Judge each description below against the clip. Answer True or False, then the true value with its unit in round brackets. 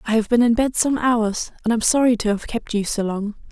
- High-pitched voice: True (225 Hz)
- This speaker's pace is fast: True (275 wpm)